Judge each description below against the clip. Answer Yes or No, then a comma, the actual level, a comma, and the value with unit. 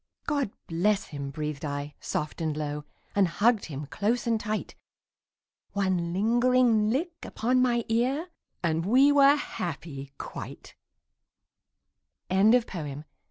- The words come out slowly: Yes, slow, 115 wpm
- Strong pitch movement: Yes, wide, 7.8 semitones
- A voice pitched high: Yes, high, 205 Hz